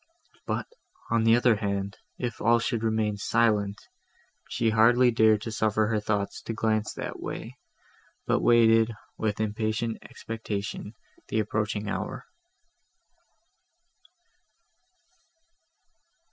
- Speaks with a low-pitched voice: Yes, low, 110 Hz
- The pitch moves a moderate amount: No, narrow, 1.4 semitones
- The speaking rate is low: Yes, slow, 105 wpm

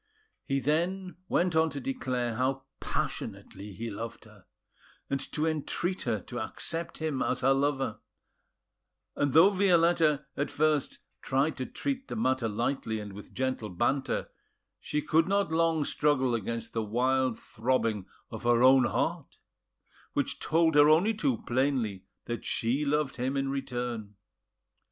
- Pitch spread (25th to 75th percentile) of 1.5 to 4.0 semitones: No, average, 4.8 semitones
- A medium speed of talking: Yes, average, 145 wpm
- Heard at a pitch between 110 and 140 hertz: Yes, low, 135 Hz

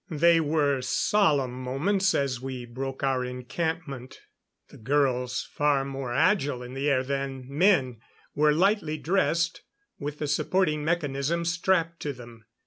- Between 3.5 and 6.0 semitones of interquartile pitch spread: Yes, average, 4.2 semitones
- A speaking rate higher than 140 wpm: No, slow, 135 wpm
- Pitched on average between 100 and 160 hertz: Yes, medium, 140 Hz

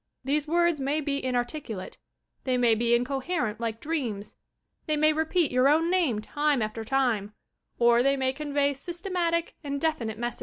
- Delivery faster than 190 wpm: No, average, 160 wpm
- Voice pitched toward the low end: No, very high, 275 Hz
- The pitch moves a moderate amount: Yes, average, 4.5 semitones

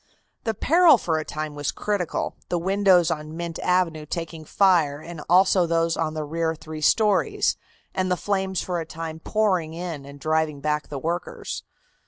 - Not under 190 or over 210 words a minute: No, average, 175 wpm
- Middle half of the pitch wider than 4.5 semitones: No, average, 2.9 semitones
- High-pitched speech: No, medium, 165 Hz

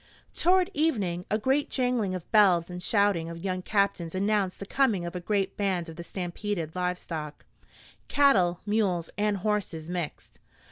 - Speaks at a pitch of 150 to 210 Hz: Yes, high, 190 Hz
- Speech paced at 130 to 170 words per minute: Yes, average, 155 wpm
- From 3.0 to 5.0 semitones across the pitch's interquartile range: Yes, average, 3.4 semitones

